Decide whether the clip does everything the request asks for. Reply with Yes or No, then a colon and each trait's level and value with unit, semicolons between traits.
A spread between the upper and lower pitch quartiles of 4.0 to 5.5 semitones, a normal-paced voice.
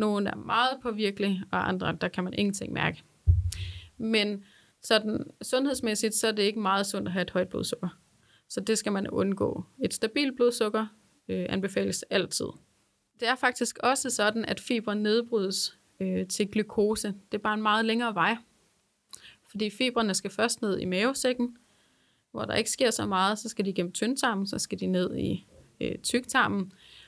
No: average, 3.3 semitones; average, 175 wpm